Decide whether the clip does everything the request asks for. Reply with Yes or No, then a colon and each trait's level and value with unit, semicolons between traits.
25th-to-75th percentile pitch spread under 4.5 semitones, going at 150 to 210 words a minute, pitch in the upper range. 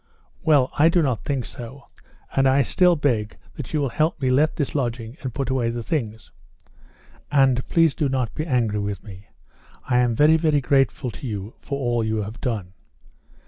No: average, 3.9 semitones; average, 190 wpm; low, 130 Hz